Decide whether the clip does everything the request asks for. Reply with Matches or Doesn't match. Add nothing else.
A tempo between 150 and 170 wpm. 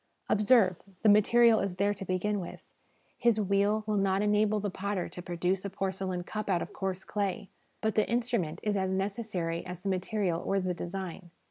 Doesn't match